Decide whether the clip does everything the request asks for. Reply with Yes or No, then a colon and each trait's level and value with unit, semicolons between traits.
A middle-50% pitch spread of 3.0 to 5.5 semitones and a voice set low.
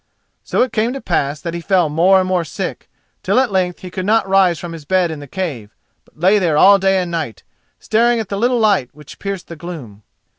No: average, 3.6 semitones; medium, 185 Hz